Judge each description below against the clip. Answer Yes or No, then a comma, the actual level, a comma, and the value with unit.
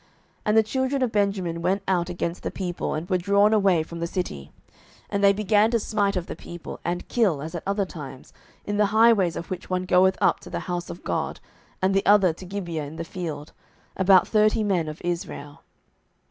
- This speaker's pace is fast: Yes, fast, 215 wpm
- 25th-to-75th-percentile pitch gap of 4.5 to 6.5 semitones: No, average, 3.2 semitones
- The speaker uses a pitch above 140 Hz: Yes, medium, 185 Hz